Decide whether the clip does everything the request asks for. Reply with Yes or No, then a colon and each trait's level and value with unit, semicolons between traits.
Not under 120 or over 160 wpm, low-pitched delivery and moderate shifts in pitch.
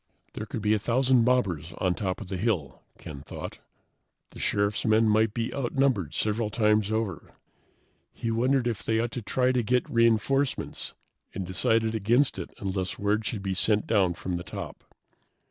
No: average, 175 wpm; low, 110 Hz; average, 3.3 semitones